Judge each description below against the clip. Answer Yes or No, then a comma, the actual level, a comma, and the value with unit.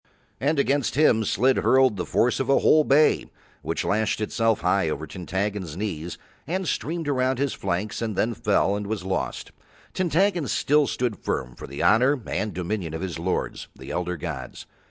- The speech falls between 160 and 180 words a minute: Yes, average, 175 wpm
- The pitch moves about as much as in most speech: No, wide, 7.0 semitones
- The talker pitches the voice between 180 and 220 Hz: No, low, 110 Hz